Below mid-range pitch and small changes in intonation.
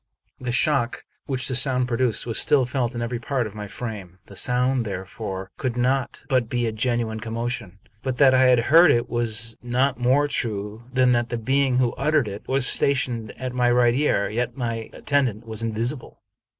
Yes: low, 120 Hz; narrow, 2.3 semitones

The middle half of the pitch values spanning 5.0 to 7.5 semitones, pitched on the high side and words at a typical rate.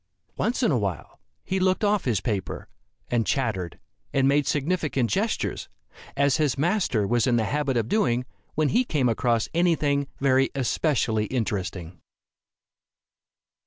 No: wide, 5.4 semitones; low, 135 Hz; average, 145 wpm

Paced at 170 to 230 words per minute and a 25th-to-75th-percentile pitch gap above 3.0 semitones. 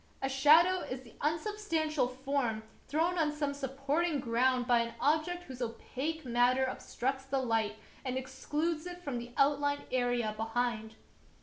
No: average, 150 wpm; average, 4.0 semitones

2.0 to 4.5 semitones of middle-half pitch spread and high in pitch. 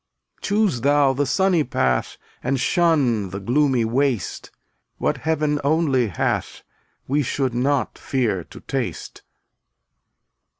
No: average, 3.6 semitones; low, 135 Hz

